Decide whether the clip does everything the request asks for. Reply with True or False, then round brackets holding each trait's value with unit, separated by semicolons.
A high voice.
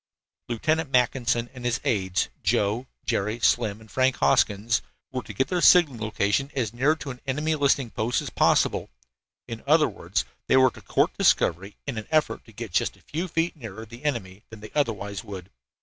False (120 Hz)